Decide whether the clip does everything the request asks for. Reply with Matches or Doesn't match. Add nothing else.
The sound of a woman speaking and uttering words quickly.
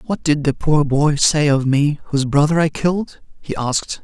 Doesn't match